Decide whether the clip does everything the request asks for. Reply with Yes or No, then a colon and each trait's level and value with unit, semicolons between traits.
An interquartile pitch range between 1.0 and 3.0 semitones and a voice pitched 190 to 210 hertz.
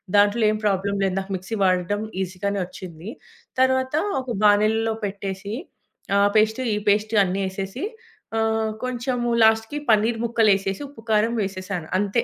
Yes: narrow, 2.5 semitones; high, 205 Hz